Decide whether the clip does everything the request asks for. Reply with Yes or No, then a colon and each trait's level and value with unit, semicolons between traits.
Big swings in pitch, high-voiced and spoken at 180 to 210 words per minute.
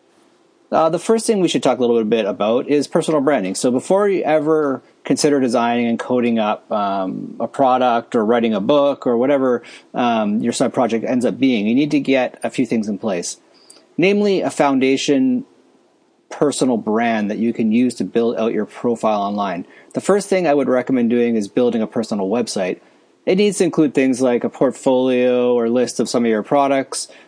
No: wide, 8.5 semitones; low, 130 Hz; average, 200 wpm